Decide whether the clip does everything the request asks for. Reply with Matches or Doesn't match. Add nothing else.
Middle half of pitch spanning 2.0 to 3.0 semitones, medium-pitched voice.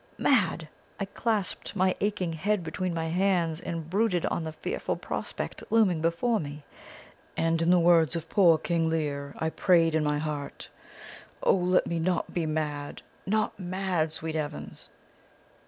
Matches